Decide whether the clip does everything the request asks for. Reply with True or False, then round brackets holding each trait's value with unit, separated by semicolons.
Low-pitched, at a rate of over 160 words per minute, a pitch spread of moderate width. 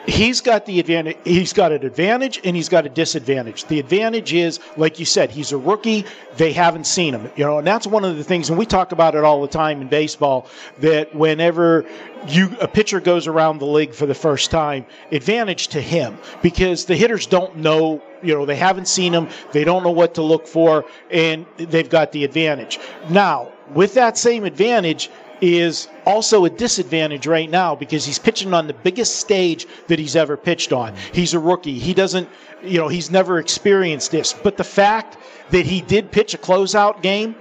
False (170 Hz; 205 wpm; 3.5 semitones)